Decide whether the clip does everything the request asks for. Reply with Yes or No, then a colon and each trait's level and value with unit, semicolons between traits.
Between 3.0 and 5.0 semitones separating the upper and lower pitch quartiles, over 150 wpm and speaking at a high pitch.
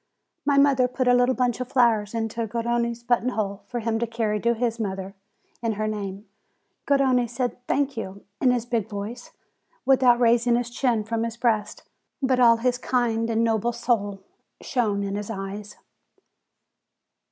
No: narrow, 2.4 semitones; average, 170 wpm; high, 235 Hz